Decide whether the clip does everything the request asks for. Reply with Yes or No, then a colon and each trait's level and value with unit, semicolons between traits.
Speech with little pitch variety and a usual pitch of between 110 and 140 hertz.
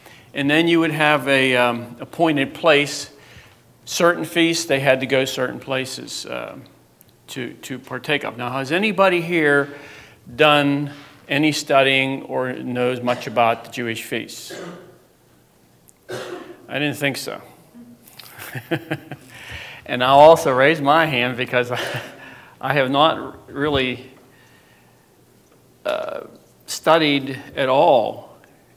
No: average, 3.2 semitones; low, 135 Hz